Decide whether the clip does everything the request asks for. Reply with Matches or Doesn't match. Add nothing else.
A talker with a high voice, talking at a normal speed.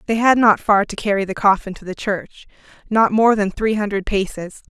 Doesn't match